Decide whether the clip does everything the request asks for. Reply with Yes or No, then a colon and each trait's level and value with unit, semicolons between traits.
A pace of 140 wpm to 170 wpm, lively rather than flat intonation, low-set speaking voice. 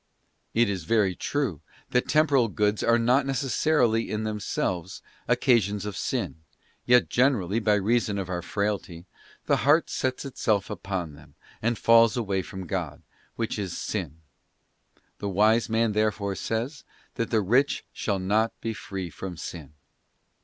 No: average, 155 wpm; average, 3.5 semitones; low, 105 Hz